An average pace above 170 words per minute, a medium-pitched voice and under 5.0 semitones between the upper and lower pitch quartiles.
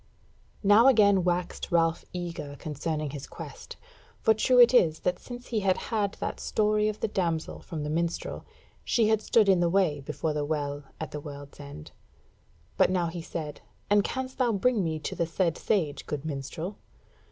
No: average, 185 wpm; medium, 175 Hz; wide, 5.5 semitones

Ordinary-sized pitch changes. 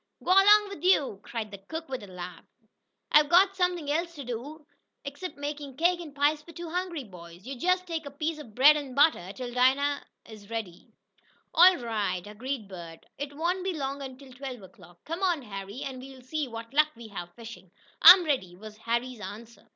No: wide, 6.5 semitones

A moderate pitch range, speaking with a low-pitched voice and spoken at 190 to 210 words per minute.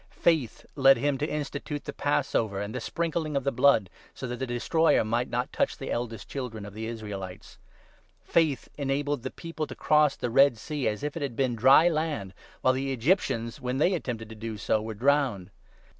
Yes: average, 4.4 semitones; low, 130 Hz; fast, 205 wpm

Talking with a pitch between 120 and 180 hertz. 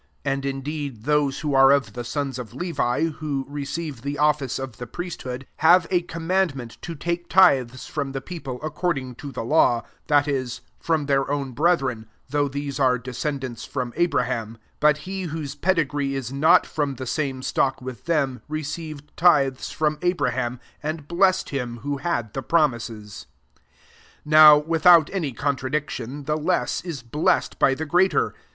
Yes: medium, 140 Hz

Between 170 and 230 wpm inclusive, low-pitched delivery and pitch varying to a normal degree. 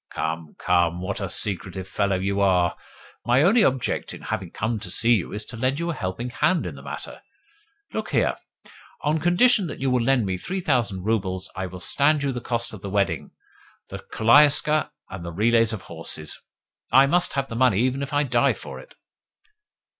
No: average, 200 wpm; low, 115 Hz; wide, 6.6 semitones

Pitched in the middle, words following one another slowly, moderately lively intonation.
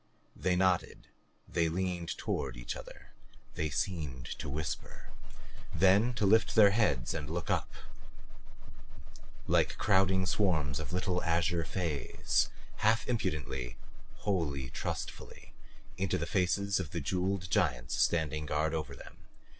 No: very low, 85 Hz; slow, 125 wpm; average, 4.1 semitones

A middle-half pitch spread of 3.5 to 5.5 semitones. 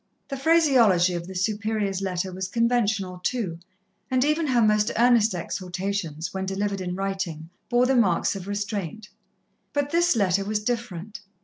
Yes: average, 4.3 semitones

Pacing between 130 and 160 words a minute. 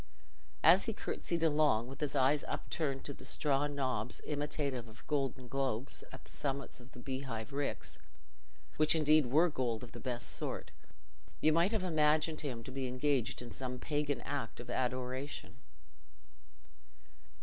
Yes: average, 155 wpm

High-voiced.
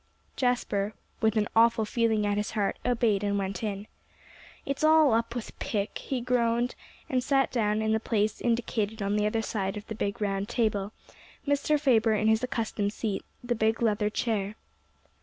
Yes: high, 220 Hz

